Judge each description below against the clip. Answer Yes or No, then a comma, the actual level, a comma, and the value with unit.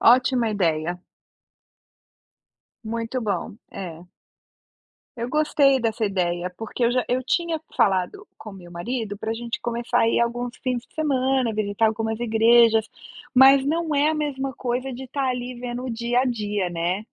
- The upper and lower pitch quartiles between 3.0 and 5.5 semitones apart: Yes, average, 3.3 semitones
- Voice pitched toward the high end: Yes, high, 235 Hz